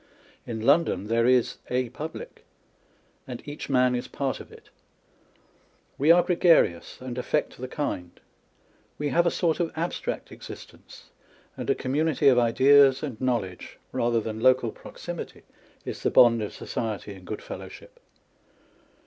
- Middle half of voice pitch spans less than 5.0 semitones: Yes, average, 4.2 semitones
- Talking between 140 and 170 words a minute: Yes, average, 150 wpm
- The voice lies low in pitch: Yes, low, 130 Hz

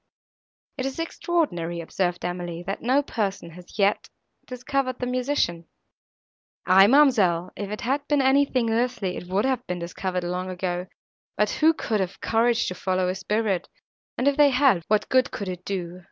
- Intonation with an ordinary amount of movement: No, wide, 6.2 semitones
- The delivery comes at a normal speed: Yes, average, 170 wpm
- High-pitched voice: Yes, high, 205 Hz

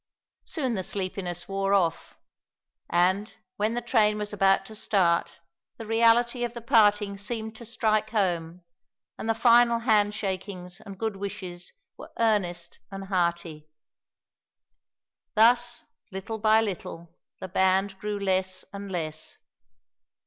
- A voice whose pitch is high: Yes, high, 200 Hz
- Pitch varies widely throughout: No, average, 3.1 semitones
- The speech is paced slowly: Yes, slow, 125 wpm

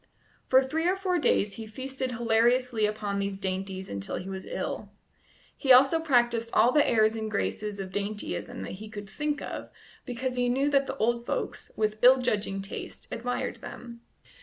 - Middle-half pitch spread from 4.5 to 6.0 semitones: No, average, 3.9 semitones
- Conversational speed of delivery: Yes, average, 180 wpm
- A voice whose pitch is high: Yes, high, 235 Hz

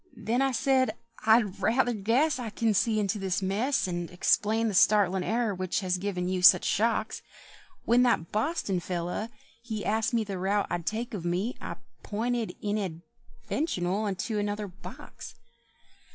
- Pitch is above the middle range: Yes, high, 210 Hz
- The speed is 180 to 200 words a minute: No, average, 150 wpm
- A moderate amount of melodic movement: Yes, average, 3.7 semitones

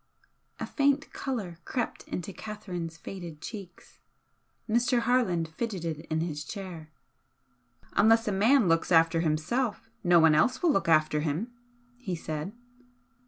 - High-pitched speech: No, medium, 180 Hz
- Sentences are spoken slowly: Yes, slow, 130 wpm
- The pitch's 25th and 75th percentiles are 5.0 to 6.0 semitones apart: Yes, wide, 5.6 semitones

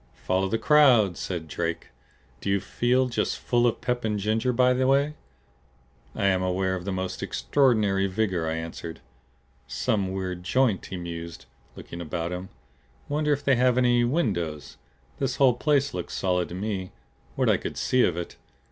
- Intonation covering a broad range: Yes, wide, 5.8 semitones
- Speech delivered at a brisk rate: No, average, 175 wpm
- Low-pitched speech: Yes, low, 100 Hz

